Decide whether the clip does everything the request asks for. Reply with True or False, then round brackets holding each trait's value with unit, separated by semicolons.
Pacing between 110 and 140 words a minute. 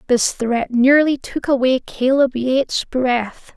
True (135 wpm)